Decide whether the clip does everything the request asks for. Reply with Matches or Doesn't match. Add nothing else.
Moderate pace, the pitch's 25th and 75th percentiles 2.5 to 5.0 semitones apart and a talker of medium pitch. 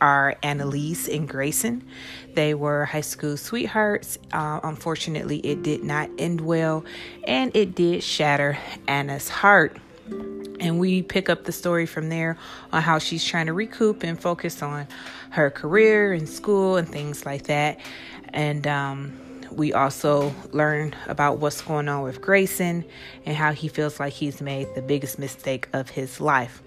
Matches